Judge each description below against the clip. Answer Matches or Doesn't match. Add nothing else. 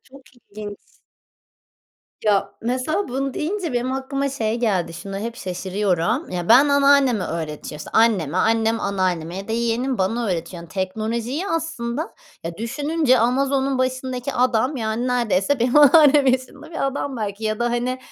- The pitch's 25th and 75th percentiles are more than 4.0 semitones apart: Matches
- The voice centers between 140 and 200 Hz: Doesn't match